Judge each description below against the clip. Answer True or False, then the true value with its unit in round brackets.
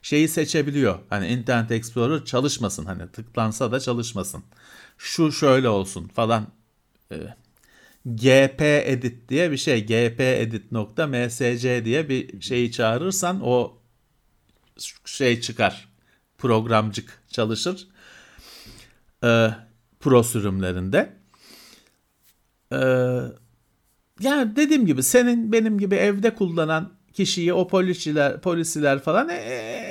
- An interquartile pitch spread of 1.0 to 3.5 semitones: False (5.6 semitones)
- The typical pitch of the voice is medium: False (125 Hz)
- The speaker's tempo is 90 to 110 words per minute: True (100 wpm)